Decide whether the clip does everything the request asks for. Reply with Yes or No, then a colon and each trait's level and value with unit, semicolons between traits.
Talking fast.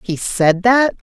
No: average, 160 wpm